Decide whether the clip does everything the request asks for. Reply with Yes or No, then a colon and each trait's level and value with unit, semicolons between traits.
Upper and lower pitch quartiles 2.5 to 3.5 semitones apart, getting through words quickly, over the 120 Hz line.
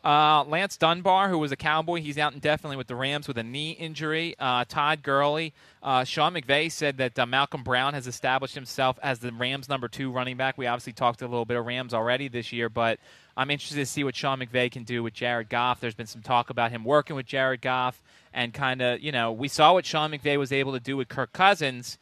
Yes: average, 3.2 semitones; fast, 245 wpm; low, 135 Hz